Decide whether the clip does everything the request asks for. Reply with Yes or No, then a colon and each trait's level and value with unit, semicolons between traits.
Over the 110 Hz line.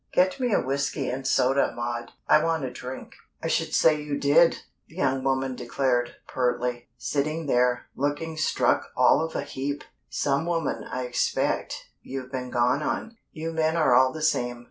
Yes: low, 135 Hz